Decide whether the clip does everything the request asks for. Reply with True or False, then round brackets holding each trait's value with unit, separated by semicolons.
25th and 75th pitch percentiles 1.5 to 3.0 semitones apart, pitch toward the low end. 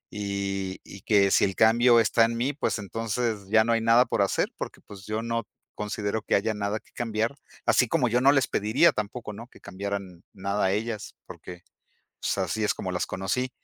True (2.7 semitones; 110 Hz)